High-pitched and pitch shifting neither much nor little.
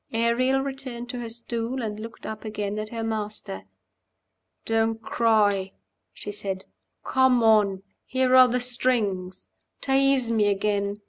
Yes: high, 225 Hz; average, 3.1 semitones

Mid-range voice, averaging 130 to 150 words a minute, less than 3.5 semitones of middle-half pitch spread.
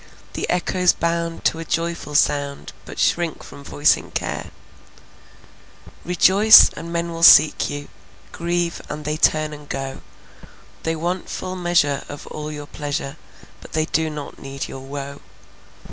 Yes: medium, 155 Hz; average, 145 wpm; average, 2.8 semitones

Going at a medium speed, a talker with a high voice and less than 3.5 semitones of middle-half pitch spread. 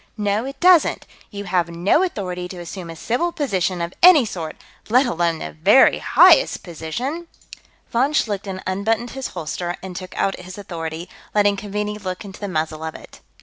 No: average, 175 wpm; high, 195 Hz; average, 4.6 semitones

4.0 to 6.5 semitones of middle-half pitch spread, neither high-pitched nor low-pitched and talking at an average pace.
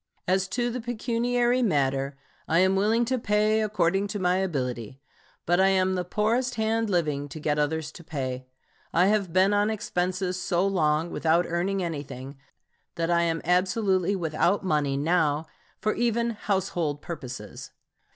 Yes: average, 5.2 semitones; medium, 180 Hz; average, 155 wpm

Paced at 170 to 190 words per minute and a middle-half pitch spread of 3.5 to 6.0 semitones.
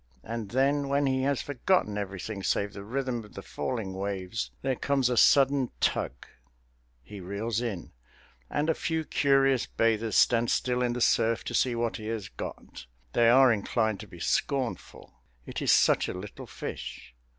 Yes: average, 175 wpm; average, 4.4 semitones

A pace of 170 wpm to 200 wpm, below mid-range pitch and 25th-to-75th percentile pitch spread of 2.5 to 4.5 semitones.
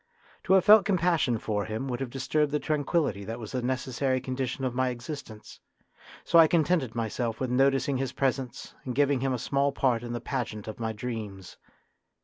Yes: average, 190 wpm; low, 130 Hz; average, 3.1 semitones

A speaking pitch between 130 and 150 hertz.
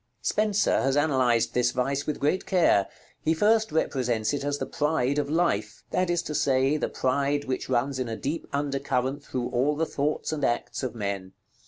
Yes: medium, 140 Hz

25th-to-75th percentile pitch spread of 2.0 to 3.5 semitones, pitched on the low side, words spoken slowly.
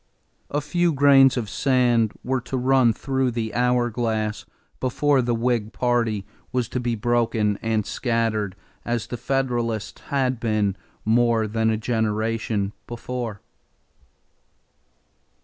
Yes: narrow, 2.4 semitones; low, 120 Hz; slow, 125 wpm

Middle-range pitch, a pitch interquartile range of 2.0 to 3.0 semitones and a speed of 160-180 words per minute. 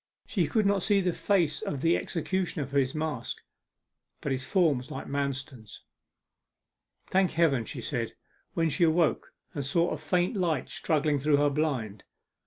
No: medium, 155 Hz; average, 4.0 semitones; average, 165 wpm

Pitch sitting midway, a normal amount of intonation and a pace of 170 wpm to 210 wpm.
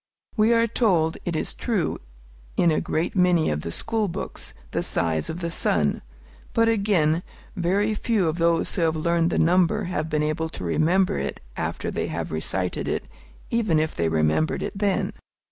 Yes: medium, 170 Hz; average, 4.3 semitones; average, 180 wpm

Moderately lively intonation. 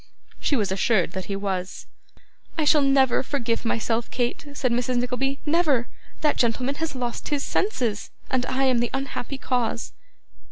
Yes: average, 3.1 semitones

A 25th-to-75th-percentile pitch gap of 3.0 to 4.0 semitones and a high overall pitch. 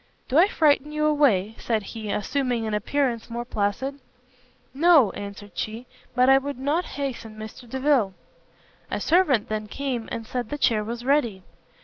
No: average, 4.7 semitones; high, 245 Hz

